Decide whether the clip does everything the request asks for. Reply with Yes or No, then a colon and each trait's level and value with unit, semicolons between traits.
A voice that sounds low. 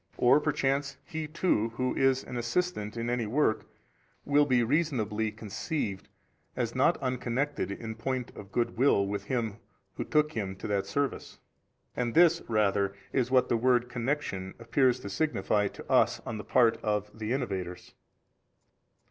Yes: low, 120 Hz